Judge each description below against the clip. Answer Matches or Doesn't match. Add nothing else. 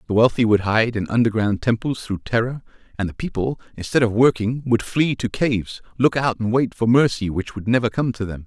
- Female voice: Doesn't match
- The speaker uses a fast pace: Matches